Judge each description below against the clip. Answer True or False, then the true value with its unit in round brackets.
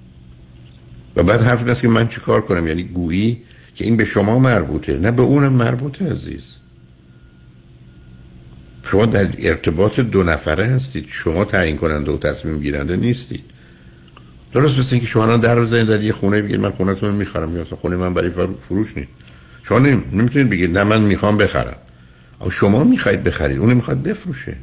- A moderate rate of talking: False (170 wpm)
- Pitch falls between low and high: False (95 Hz)